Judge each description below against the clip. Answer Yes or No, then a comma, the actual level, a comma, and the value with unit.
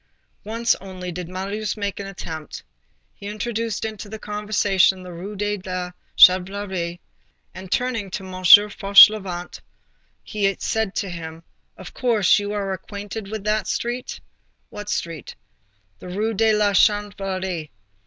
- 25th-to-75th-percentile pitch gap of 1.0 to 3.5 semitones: Yes, narrow, 2.4 semitones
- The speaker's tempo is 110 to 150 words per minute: Yes, slow, 135 wpm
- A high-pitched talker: Yes, high, 200 Hz